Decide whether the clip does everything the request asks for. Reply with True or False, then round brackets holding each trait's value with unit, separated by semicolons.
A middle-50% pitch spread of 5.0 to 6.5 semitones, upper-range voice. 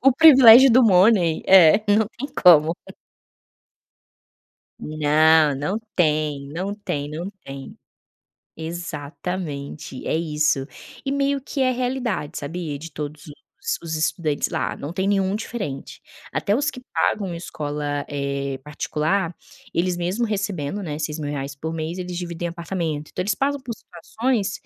False (5.4 semitones; 170 Hz)